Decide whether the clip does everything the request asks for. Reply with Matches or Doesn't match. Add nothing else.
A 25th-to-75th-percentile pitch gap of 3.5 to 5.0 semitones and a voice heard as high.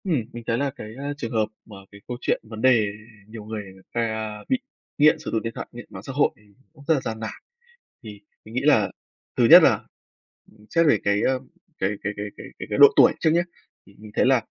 Doesn't match